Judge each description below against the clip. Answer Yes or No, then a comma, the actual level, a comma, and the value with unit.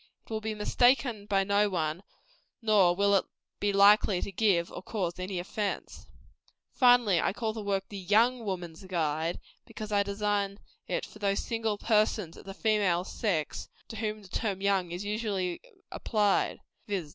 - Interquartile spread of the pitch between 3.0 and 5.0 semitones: No, narrow, 2.5 semitones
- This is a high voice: Yes, high, 200 Hz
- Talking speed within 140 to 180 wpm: Yes, average, 170 wpm